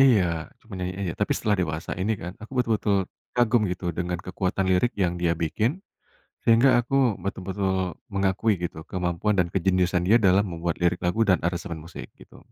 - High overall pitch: No, very low, 95 Hz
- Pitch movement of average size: Yes, average, 3.4 semitones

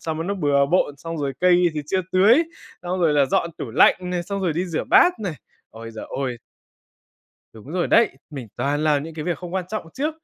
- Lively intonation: No, average, 4.4 semitones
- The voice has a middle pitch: Yes, medium, 165 Hz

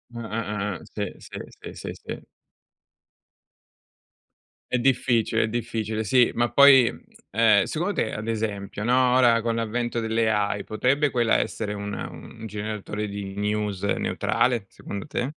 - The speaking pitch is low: Yes, low, 110 Hz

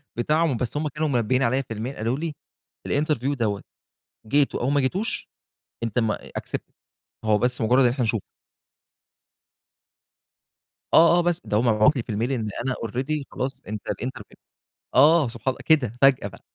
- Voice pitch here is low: Yes, low, 130 Hz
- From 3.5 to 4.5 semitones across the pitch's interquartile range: Yes, average, 4.0 semitones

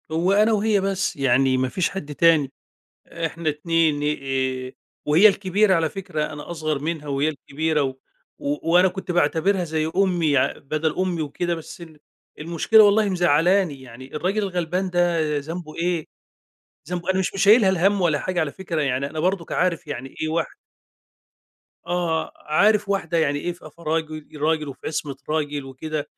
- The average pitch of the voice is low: No, medium, 165 Hz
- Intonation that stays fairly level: No, average, 3.5 semitones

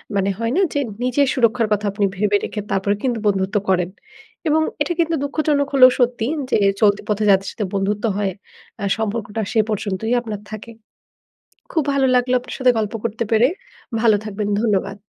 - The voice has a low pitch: No, high, 220 Hz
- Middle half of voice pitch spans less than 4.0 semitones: Yes, average, 3.6 semitones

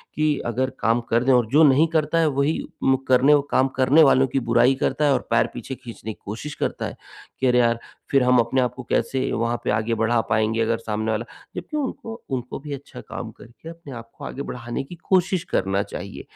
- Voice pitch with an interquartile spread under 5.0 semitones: Yes, average, 3.5 semitones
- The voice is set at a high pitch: No, low, 125 Hz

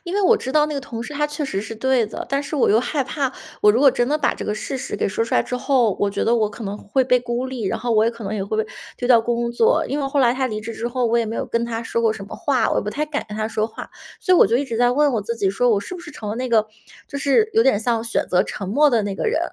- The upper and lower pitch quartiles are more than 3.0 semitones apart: Yes, average, 3.9 semitones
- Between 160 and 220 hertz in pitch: No, high, 240 Hz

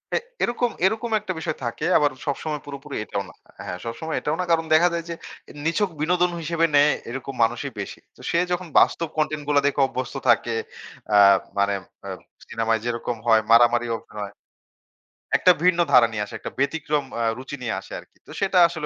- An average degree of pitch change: No, wide, 6.1 semitones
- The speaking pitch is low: No, medium, 145 Hz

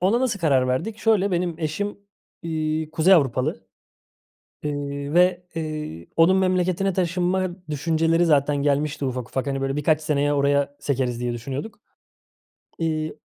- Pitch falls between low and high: Yes, medium, 155 Hz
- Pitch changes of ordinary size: Yes, average, 4.1 semitones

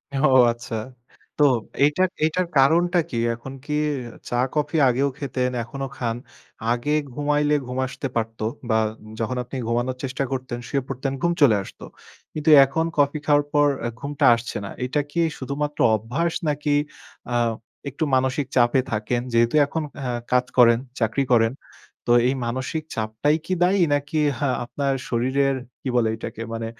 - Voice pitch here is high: No, low, 135 Hz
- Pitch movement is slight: No, average, 3.5 semitones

